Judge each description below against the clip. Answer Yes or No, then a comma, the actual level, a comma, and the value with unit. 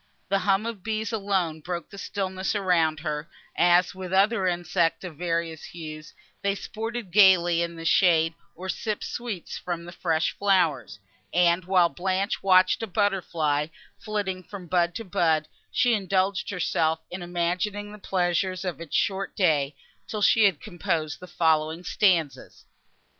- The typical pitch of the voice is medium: Yes, medium, 180 Hz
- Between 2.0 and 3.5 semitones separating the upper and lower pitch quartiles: Yes, average, 2.8 semitones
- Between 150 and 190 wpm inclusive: Yes, average, 155 wpm